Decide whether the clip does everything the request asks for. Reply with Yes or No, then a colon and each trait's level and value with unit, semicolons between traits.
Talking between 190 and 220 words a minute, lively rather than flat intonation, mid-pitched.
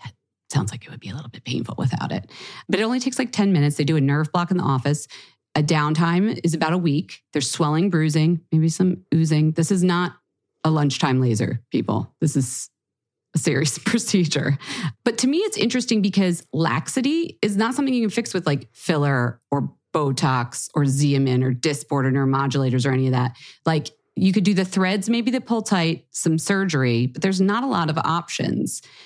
Yes: average, 200 wpm; wide, 5.7 semitones; medium, 160 Hz